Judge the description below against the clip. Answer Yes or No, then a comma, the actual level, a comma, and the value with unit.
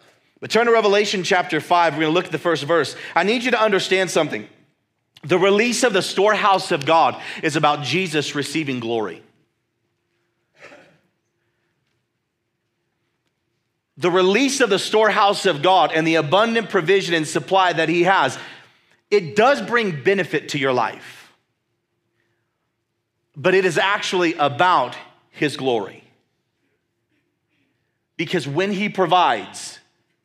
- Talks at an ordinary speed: No, slow, 130 wpm